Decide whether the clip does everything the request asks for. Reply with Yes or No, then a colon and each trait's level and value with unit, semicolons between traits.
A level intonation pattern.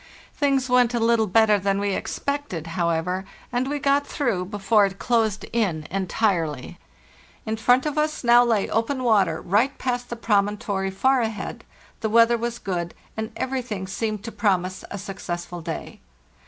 No: average, 4.2 semitones